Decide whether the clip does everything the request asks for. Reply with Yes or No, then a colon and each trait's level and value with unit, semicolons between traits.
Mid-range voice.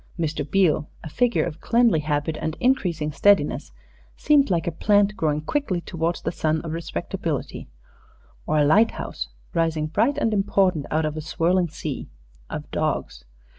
Yes: medium, 165 Hz